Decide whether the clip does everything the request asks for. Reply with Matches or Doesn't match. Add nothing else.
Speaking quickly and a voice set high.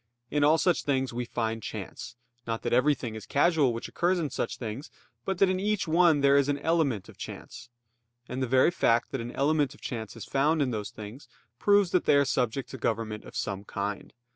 Doesn't match